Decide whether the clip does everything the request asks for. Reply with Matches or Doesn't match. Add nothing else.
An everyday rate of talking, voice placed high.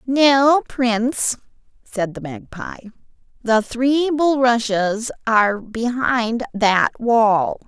Doesn't match